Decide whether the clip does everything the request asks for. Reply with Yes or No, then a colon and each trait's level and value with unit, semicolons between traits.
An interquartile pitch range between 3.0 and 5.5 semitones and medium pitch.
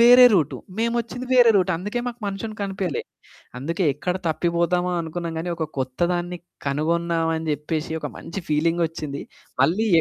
Yes: average, 3.6 semitones; medium, 170 Hz